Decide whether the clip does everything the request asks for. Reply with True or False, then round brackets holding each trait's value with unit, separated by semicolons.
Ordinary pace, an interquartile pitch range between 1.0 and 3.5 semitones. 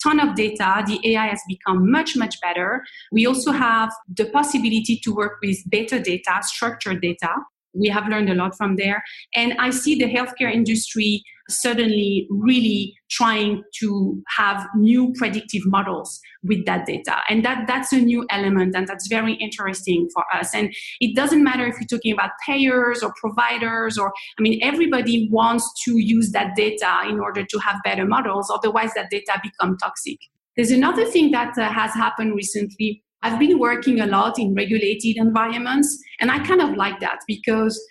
True (175 wpm; 2.9 semitones)